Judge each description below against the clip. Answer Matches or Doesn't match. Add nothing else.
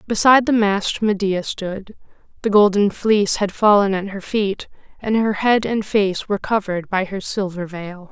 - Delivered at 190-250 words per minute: Doesn't match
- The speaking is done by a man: Doesn't match